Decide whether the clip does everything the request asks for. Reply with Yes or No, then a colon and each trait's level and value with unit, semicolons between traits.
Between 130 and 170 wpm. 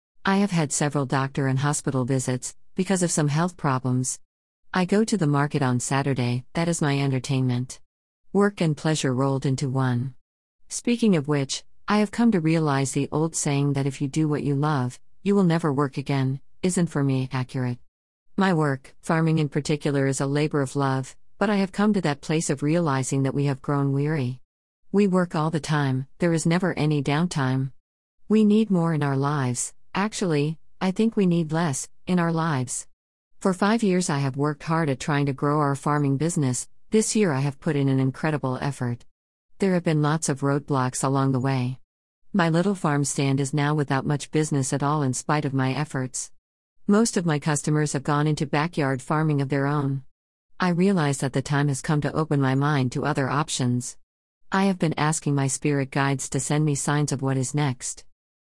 No: average, 200 wpm